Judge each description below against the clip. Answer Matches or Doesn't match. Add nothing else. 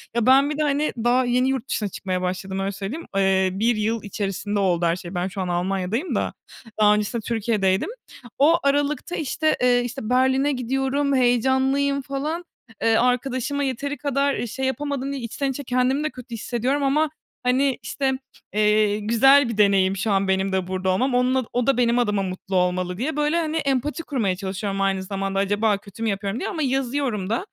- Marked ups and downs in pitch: Matches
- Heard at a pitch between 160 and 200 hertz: Doesn't match